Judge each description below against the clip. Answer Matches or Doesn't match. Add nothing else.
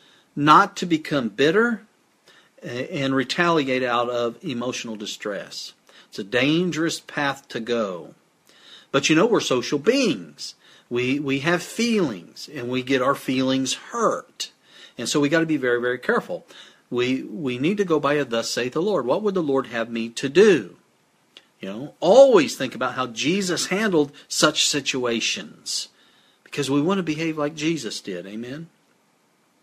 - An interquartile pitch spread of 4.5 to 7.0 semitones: Matches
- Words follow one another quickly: Doesn't match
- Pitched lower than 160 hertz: Matches